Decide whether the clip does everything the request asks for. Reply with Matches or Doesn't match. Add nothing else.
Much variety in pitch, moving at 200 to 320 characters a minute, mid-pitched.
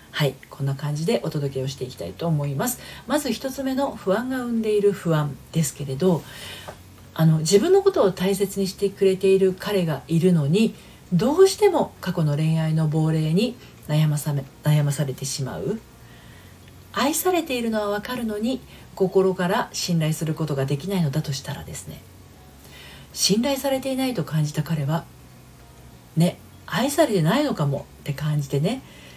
Doesn't match